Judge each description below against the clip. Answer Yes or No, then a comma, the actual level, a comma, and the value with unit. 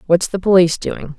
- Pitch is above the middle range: No, medium, 175 Hz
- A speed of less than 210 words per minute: Yes, average, 200 wpm